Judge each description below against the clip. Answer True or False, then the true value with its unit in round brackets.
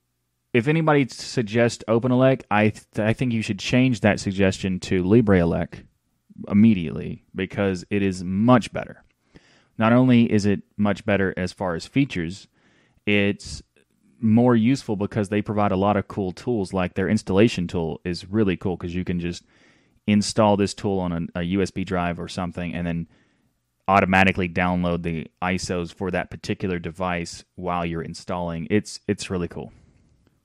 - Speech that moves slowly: False (160 wpm)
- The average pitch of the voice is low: True (95 Hz)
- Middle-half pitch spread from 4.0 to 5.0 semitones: False (3.3 semitones)